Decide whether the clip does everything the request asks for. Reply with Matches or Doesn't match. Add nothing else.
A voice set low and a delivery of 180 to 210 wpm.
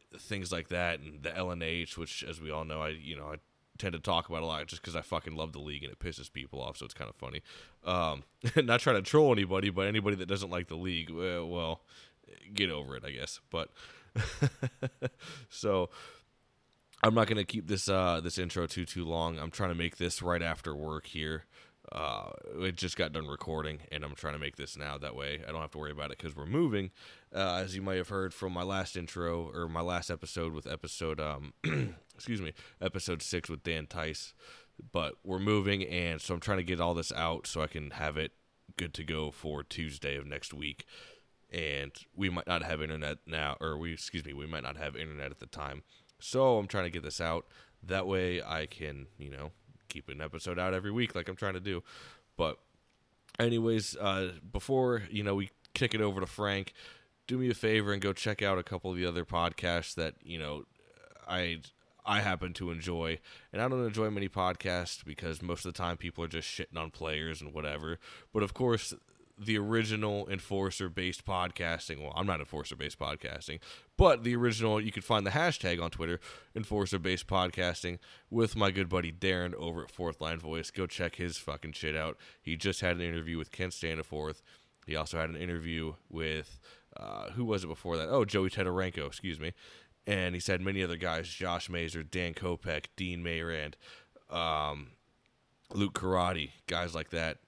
Matches